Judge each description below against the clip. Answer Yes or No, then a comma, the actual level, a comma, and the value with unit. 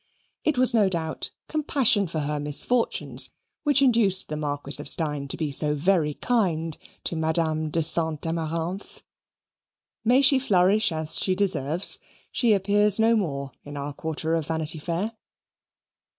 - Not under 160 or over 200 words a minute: No, average, 150 wpm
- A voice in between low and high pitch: Yes, medium, 165 Hz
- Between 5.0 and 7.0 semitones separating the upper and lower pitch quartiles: Yes, wide, 5.4 semitones